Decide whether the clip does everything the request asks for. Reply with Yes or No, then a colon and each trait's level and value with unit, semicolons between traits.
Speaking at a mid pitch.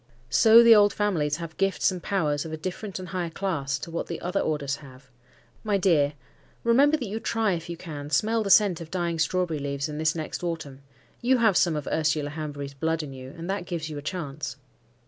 Yes: medium, 165 Hz